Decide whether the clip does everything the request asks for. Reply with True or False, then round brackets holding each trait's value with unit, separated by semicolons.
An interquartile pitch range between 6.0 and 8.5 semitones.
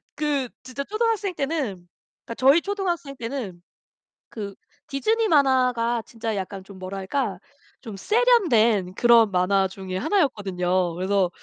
True (7.1 semitones)